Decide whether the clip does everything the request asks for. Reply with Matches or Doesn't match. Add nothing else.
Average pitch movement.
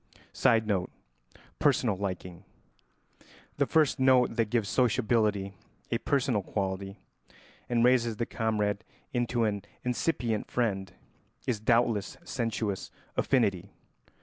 Matches